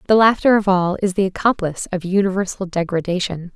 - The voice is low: No, high, 190 Hz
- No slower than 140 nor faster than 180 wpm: Yes, average, 170 wpm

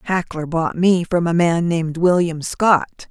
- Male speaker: No, female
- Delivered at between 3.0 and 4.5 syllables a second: Yes, 4.1 syllables/s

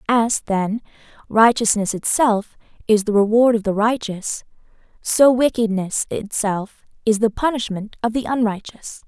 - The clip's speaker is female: Yes, female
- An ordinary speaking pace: No, slow, 125 wpm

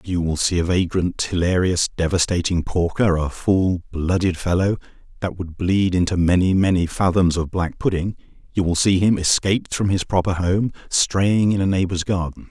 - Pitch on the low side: Yes, very low, 90 Hz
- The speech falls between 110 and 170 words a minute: Yes, average, 165 wpm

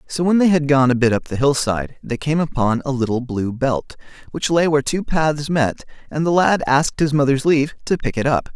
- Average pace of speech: No, fast, 245 wpm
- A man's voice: Yes, male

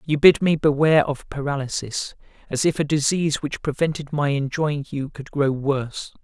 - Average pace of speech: Yes, average, 175 wpm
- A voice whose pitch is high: No, medium, 145 Hz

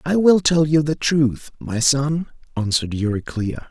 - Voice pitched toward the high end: No, medium, 140 Hz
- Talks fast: No, average, 160 wpm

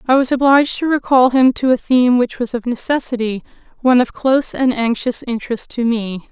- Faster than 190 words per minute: Yes, average, 200 wpm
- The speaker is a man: No, female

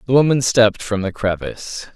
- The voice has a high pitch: No, low, 110 Hz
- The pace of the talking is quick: No, average, 185 wpm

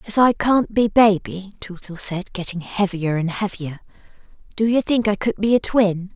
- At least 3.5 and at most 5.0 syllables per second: Yes, 4.7 syllables/s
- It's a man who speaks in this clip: No, female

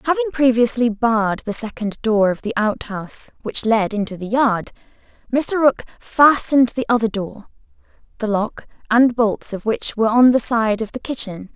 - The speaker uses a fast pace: No, average, 170 wpm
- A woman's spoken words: Yes, female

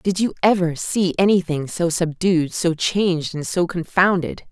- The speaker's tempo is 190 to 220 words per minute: No, average, 160 wpm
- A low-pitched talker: No, medium, 175 Hz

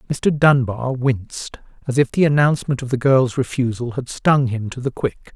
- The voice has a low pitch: Yes, low, 130 Hz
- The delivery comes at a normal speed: Yes, average, 190 wpm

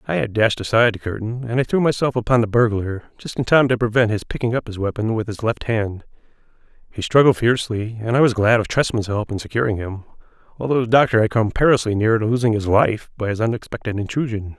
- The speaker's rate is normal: No, fast, 225 wpm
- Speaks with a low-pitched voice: Yes, low, 115 Hz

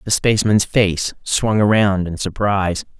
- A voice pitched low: Yes, low, 100 Hz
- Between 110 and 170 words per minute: Yes, average, 140 wpm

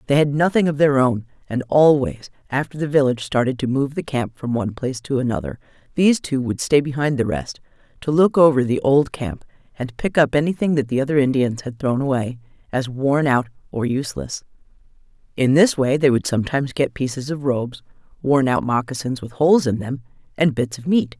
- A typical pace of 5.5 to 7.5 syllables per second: Yes, 5.7 syllables/s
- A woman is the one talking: Yes, female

